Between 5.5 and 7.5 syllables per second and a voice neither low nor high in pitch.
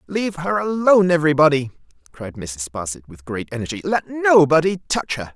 Yes: 5.6 syllables/s; medium, 150 Hz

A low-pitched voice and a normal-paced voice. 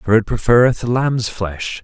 Yes: low, 115 Hz; average, 165 wpm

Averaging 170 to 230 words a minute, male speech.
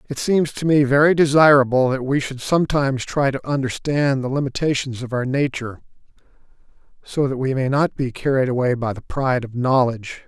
Yes: average, 180 wpm; male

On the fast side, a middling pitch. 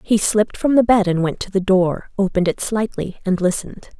No: fast, 225 wpm; high, 200 Hz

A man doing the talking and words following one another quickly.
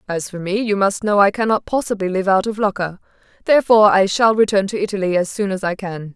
No: female; fast, 235 wpm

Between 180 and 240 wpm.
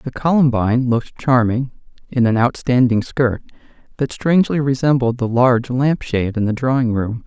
No: average, 155 wpm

